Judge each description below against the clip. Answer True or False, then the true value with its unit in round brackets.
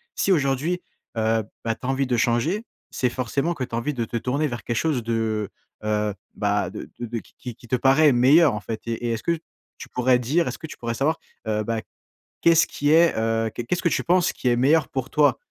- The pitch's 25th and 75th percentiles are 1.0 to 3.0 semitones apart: False (4.7 semitones)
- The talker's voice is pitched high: False (125 Hz)